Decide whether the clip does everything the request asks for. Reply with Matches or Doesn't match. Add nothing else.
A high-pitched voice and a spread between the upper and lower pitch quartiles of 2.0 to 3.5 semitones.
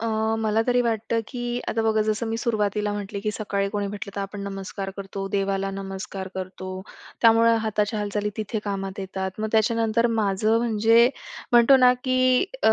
Matches